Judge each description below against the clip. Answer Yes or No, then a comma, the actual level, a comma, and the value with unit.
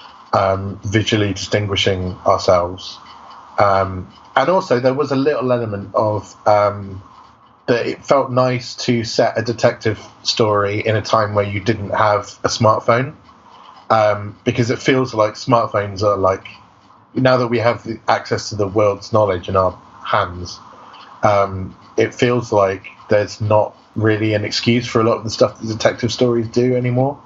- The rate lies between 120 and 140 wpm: No, average, 160 wpm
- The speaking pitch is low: Yes, low, 110 Hz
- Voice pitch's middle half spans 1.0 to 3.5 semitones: Yes, average, 2.9 semitones